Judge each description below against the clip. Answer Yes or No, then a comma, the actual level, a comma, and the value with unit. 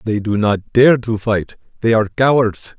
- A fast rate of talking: No, average, 195 wpm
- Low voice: Yes, low, 110 Hz